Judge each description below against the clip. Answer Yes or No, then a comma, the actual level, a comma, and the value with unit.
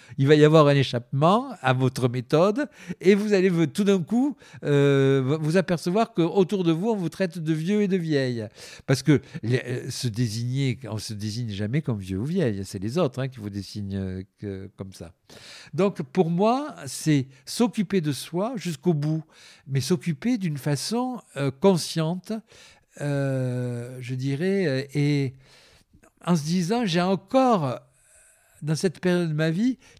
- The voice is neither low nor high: Yes, medium, 155 Hz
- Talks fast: No, average, 165 wpm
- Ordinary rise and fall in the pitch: No, wide, 6.6 semitones